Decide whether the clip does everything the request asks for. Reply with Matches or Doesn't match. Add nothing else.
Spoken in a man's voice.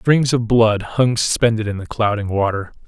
Matches